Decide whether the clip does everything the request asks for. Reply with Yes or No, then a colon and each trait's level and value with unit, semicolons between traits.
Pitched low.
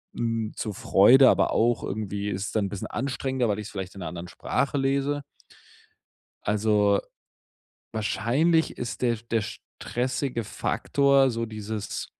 Yes: low, 115 Hz